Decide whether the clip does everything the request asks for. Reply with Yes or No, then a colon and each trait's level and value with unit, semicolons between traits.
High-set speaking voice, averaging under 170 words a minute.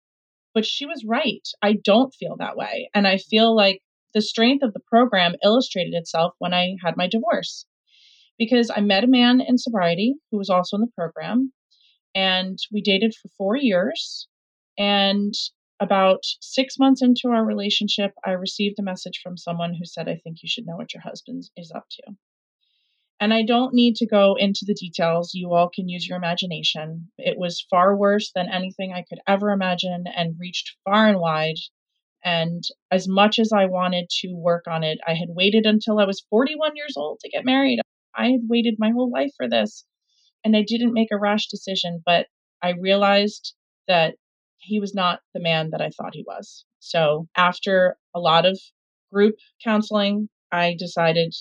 No: high, 200 Hz; average, 185 wpm